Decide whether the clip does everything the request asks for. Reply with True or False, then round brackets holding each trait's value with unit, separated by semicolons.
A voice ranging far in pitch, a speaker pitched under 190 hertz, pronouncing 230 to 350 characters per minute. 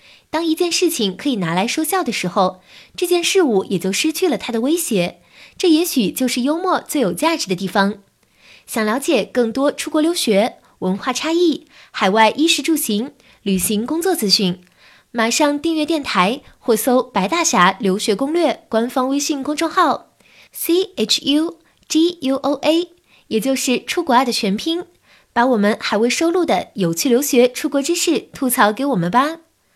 False (6.9 semitones; 265 Hz; 255 characters per minute)